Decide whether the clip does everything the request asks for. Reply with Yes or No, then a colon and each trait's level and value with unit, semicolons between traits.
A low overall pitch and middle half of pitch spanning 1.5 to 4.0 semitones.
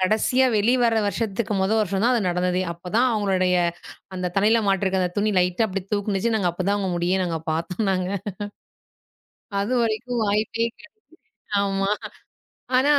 No: high, 200 Hz; average, 3.4 semitones